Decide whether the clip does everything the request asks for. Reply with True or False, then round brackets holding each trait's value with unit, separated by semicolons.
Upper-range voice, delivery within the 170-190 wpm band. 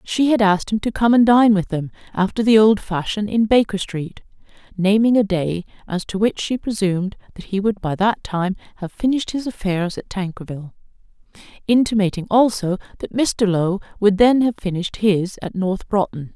True (200 Hz; 185 wpm)